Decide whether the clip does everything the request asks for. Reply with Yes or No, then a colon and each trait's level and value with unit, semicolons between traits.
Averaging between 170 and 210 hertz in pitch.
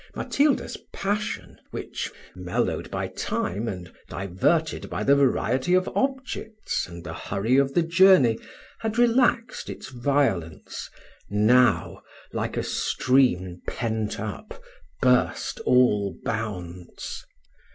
No: low, 125 Hz